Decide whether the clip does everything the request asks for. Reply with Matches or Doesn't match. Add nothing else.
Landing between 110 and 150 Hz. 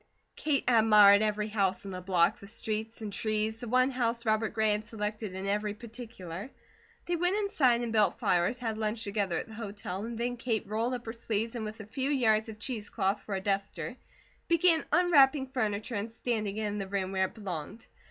Doesn't match